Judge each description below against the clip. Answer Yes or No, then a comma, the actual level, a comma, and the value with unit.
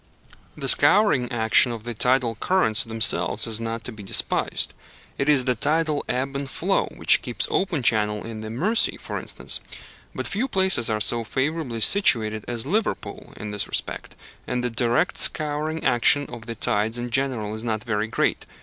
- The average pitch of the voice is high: No, low, 120 Hz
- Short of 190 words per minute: Yes, average, 175 wpm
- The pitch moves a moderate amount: Yes, average, 4.7 semitones